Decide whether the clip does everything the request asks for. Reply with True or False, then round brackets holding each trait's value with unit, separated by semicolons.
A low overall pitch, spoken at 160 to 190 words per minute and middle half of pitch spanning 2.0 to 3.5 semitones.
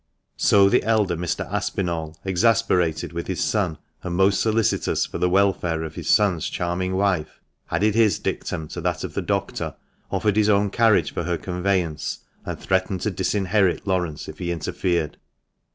True (95 Hz; 165 wpm; 2.7 semitones)